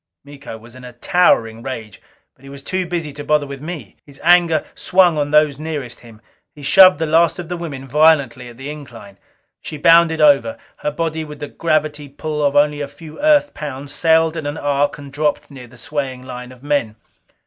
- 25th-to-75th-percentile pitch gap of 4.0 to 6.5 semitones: No, average, 3.3 semitones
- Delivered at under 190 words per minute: No, fast, 205 wpm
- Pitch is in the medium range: Yes, medium, 145 Hz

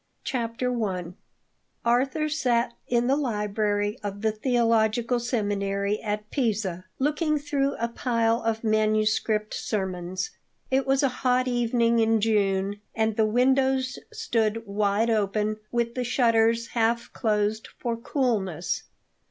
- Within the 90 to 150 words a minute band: Yes, slow, 135 wpm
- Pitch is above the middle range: Yes, high, 225 Hz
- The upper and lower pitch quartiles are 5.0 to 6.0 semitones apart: No, average, 2.8 semitones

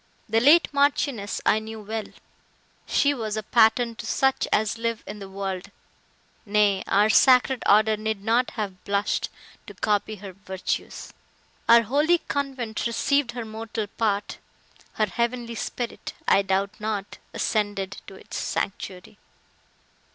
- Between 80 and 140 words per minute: Yes, slow, 135 wpm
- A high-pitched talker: Yes, high, 220 Hz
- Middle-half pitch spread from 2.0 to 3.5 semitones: Yes, average, 2.8 semitones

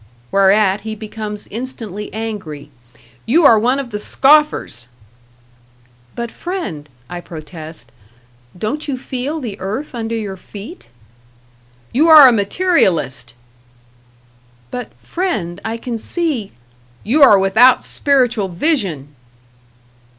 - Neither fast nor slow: No, slow, 115 wpm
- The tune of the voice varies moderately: No, wide, 5.8 semitones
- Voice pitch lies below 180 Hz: No, high, 220 Hz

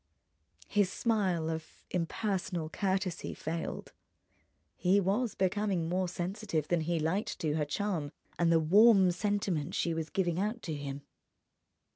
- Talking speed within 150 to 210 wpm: No, slow, 135 wpm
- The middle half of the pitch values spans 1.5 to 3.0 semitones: No, average, 3.8 semitones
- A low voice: No, medium, 180 Hz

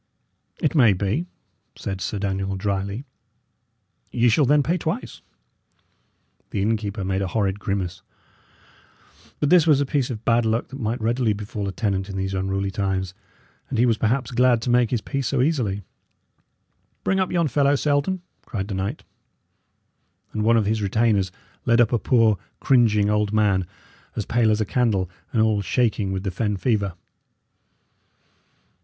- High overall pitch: No, low, 110 Hz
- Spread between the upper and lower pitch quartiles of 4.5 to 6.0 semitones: No, average, 4.0 semitones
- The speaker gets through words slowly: No, average, 165 wpm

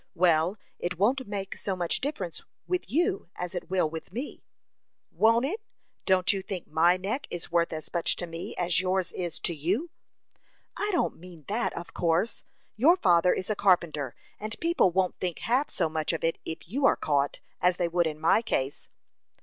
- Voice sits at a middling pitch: Yes, medium, 180 Hz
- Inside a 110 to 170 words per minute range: No, average, 190 wpm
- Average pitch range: Yes, average, 4.4 semitones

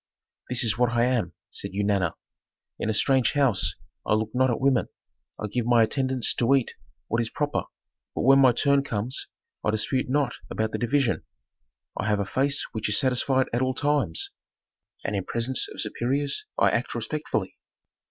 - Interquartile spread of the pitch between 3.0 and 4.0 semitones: Yes, average, 3.5 semitones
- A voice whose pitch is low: Yes, low, 120 Hz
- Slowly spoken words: No, average, 180 wpm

